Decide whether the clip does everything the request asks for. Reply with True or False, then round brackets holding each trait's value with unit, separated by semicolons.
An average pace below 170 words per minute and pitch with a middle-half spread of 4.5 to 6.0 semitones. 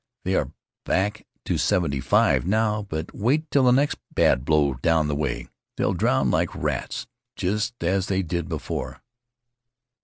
True (155 wpm; 5.6 semitones)